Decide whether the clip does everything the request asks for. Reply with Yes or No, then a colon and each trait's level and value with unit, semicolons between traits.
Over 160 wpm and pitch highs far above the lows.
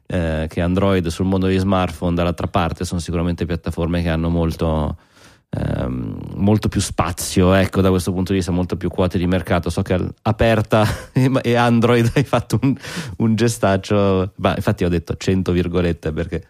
No: fast, 170 wpm; average, 3.6 semitones